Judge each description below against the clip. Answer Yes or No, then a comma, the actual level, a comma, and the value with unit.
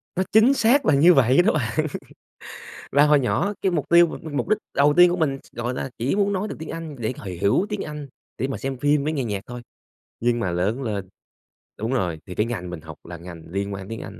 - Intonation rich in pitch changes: Yes, wide, 7.6 semitones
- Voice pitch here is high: No, low, 135 Hz